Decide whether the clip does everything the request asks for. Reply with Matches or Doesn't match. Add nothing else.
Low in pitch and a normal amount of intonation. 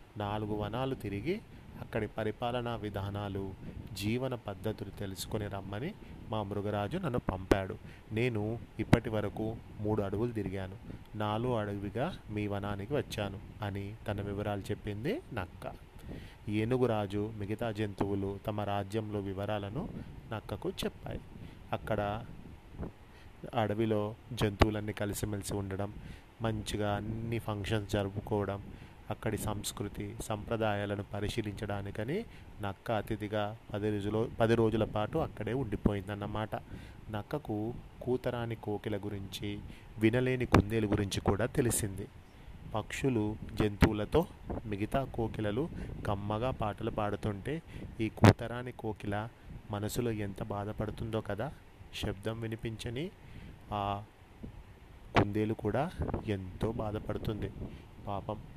Doesn't match